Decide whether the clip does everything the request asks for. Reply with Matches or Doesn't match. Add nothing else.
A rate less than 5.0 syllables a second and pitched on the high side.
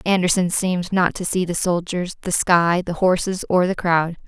Doesn't match